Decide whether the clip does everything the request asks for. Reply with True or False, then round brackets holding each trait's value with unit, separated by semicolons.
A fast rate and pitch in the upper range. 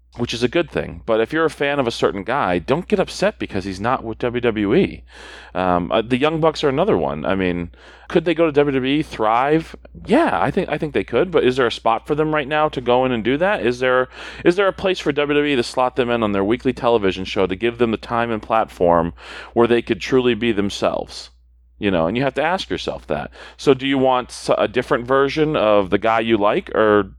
False (260 wpm; 120 Hz)